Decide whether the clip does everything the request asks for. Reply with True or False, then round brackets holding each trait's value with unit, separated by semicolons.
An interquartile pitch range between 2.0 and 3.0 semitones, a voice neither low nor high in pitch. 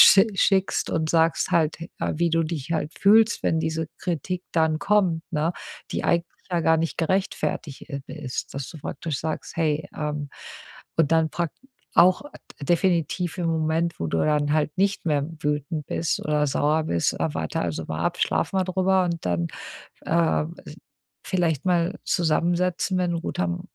True (2.7 semitones; 160 Hz)